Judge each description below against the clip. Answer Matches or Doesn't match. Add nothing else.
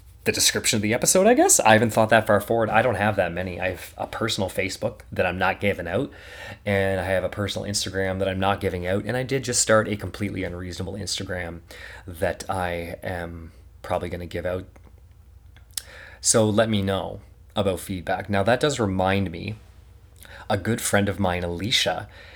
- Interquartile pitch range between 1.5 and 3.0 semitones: Matches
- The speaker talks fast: Doesn't match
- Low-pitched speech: Matches